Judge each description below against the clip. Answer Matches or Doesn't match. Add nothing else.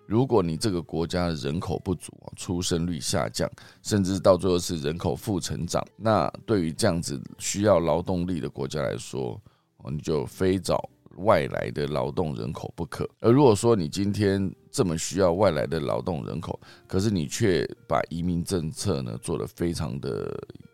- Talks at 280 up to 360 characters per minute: Doesn't match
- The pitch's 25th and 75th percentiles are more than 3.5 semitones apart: Doesn't match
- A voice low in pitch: Matches